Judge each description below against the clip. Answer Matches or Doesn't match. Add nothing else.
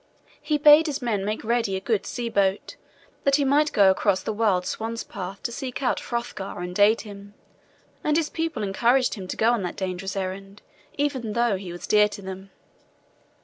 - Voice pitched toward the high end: Matches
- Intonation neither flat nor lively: Matches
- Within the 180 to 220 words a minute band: Matches